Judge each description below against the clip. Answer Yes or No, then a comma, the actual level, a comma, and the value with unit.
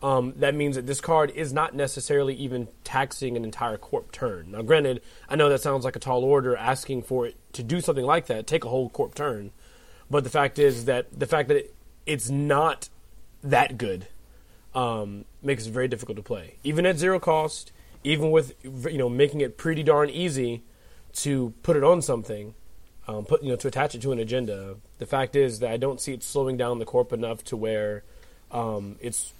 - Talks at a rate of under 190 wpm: No, fast, 205 wpm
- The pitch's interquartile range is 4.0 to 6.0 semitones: No, average, 3.6 semitones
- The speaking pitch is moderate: No, low, 130 Hz